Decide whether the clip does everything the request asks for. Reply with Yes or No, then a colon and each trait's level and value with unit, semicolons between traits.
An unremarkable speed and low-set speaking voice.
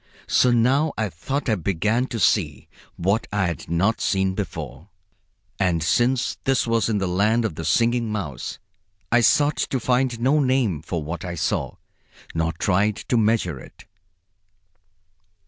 Yes: average, 155 wpm; low, 105 Hz